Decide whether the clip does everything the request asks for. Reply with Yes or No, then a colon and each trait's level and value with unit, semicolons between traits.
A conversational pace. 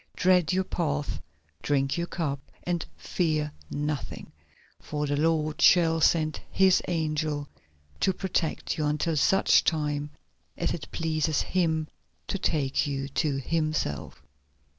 No: slow, 125 wpm